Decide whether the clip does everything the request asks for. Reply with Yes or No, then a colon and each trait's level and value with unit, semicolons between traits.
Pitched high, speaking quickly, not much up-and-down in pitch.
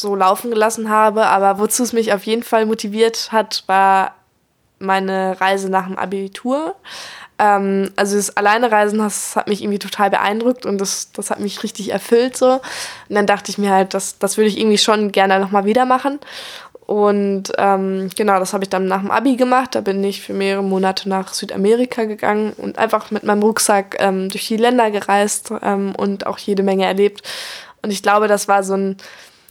Yes: high, 205 Hz; fast, 195 wpm; narrow, 2.1 semitones